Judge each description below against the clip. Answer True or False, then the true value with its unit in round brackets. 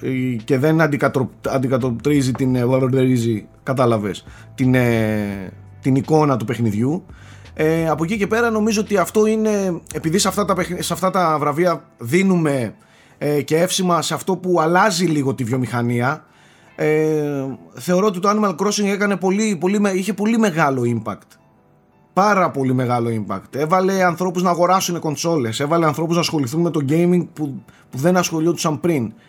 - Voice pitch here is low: False (155 Hz)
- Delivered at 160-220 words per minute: False (150 wpm)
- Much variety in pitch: True (6.0 semitones)